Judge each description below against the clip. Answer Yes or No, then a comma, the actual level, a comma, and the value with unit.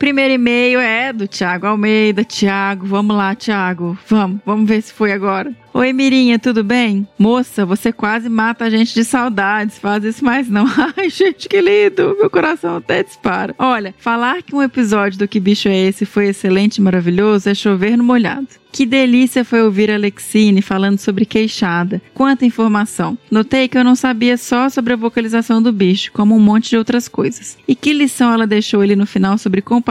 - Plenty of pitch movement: No, average, 3.6 semitones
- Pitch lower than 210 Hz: No, high, 220 Hz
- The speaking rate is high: Yes, fast, 195 wpm